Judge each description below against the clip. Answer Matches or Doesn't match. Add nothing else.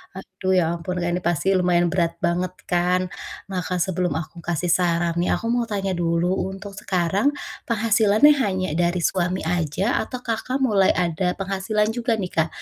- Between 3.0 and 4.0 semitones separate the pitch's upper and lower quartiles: Doesn't match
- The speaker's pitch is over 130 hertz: Matches